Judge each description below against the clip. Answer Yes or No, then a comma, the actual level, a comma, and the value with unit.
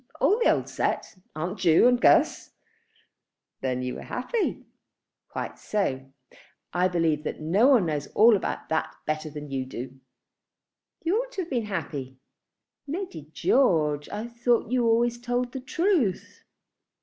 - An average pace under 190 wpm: Yes, average, 150 wpm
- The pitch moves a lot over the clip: Yes, wide, 8.4 semitones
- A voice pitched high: Yes, high, 205 Hz